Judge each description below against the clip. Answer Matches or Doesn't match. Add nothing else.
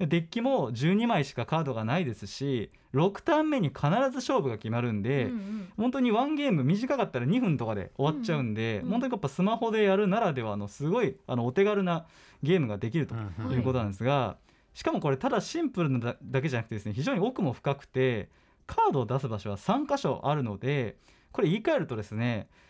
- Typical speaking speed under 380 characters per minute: Doesn't match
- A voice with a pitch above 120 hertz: Matches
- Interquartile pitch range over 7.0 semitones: Matches